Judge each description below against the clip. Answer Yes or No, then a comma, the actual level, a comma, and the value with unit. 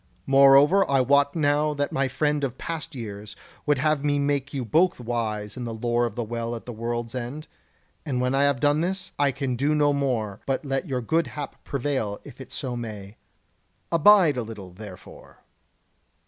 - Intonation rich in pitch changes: No, average, 3.7 semitones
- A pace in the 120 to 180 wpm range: No, average, 190 wpm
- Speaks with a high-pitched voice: No, low, 135 Hz